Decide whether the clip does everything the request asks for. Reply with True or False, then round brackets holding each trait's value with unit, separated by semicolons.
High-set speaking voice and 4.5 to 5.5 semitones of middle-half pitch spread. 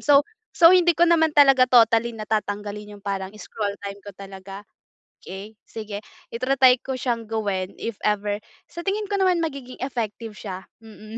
True (225 Hz; 4.9 semitones)